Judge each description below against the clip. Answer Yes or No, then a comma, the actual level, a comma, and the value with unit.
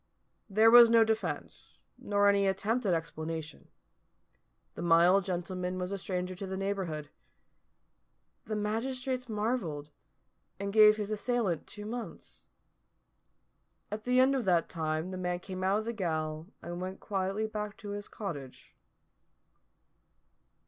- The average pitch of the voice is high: Yes, high, 195 Hz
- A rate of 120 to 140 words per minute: Yes, slow, 135 wpm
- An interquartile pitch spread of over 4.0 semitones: No, average, 3.5 semitones